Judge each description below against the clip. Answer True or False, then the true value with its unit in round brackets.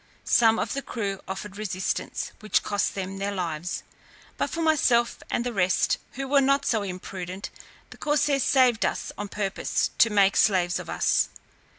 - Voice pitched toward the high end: True (205 Hz)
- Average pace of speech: True (170 wpm)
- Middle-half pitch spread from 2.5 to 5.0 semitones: True (4.5 semitones)